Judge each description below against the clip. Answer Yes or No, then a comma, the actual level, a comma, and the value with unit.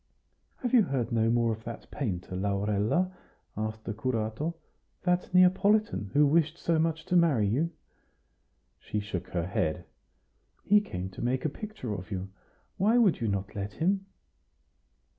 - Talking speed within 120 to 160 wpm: Yes, average, 155 wpm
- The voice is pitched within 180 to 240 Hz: No, low, 120 Hz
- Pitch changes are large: Yes, wide, 8.9 semitones